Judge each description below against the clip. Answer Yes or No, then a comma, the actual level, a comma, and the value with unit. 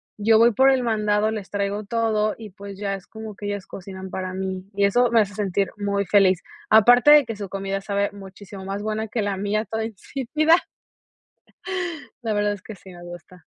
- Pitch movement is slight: Yes, narrow, 2.0 semitones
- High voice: Yes, high, 205 Hz